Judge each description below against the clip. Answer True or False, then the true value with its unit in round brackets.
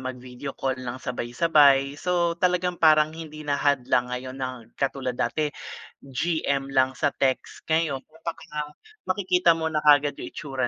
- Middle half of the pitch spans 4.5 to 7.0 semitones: False (3.6 semitones)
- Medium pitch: True (145 Hz)